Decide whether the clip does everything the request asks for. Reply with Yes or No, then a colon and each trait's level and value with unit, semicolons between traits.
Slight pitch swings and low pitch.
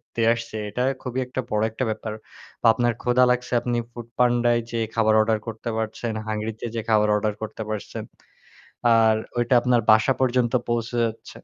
Yes: narrow, 1.7 semitones; low, 115 Hz